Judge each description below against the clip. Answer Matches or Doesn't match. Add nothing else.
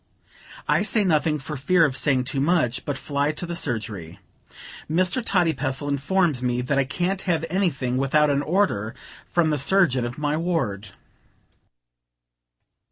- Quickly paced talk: Doesn't match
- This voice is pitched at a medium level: Matches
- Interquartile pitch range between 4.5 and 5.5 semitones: Matches